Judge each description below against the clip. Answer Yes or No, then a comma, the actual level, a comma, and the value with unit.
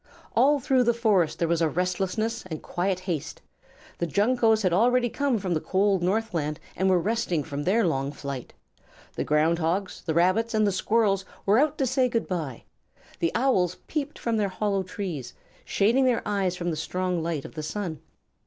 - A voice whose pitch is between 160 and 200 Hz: Yes, high, 190 Hz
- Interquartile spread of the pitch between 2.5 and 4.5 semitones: No, average, 5.0 semitones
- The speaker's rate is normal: Yes, average, 185 wpm